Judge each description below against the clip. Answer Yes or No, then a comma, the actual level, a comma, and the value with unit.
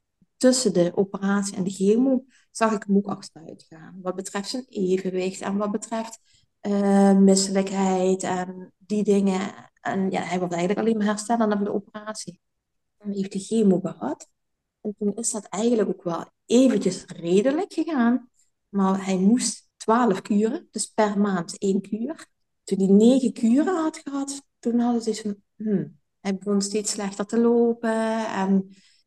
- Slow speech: No, average, 165 wpm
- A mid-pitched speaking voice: No, high, 205 Hz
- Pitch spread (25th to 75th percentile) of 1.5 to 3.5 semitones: Yes, average, 2.8 semitones